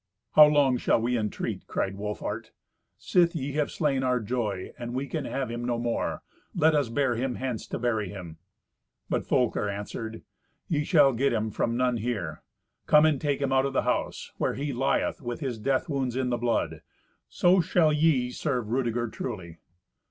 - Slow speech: No, average, 185 wpm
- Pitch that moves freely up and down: No, average, 3.5 semitones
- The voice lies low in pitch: Yes, low, 125 Hz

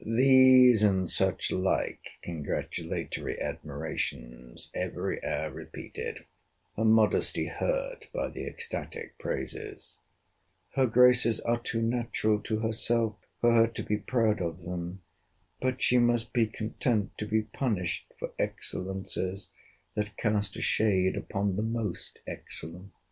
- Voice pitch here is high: No, low, 110 Hz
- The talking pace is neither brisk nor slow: No, slow, 120 wpm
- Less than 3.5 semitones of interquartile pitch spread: No, average, 3.8 semitones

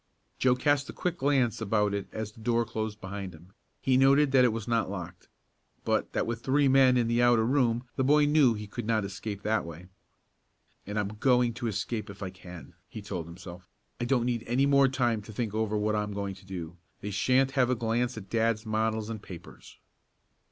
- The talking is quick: Yes, fast, 215 wpm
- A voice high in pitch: No, low, 110 Hz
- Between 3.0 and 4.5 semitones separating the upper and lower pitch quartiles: Yes, average, 3.6 semitones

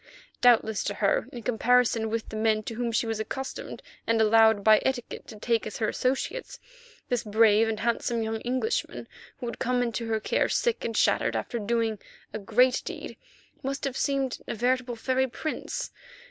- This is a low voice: No, high, 230 Hz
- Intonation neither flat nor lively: No, narrow, 2.3 semitones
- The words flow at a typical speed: Yes, average, 190 wpm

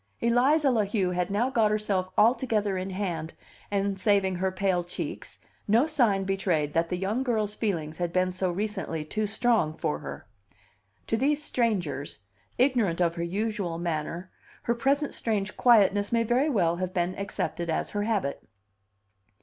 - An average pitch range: Yes, average, 4.2 semitones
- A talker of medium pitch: No, high, 200 Hz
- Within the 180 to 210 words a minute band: No, average, 160 wpm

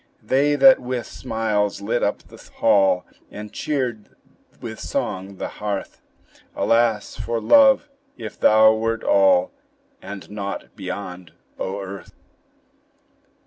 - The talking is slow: Yes, slow, 115 wpm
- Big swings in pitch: No, average, 4.2 semitones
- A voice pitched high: No, low, 110 Hz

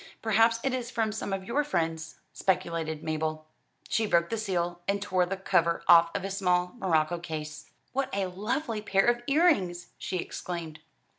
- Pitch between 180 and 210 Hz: Yes, medium, 185 Hz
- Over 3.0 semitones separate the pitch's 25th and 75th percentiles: Yes, average, 4.6 semitones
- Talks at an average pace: Yes, average, 165 wpm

